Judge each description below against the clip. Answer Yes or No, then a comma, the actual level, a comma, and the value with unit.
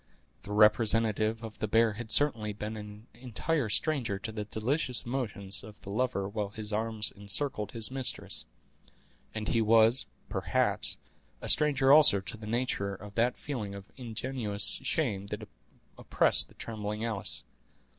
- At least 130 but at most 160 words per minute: Yes, average, 150 wpm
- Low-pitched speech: Yes, low, 110 Hz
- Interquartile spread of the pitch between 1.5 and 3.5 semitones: Yes, average, 2.7 semitones